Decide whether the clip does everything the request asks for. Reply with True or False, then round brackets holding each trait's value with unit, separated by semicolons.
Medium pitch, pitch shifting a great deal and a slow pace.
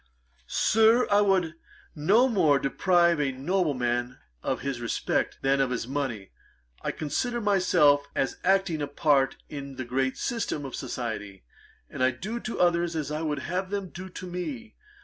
False (150 Hz; 6.0 semitones; 170 wpm)